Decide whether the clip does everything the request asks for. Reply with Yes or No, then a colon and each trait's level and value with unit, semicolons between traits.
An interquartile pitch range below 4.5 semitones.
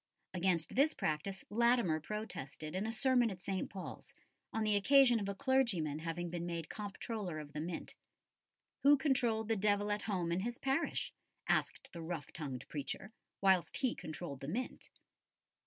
No: wide, 5.5 semitones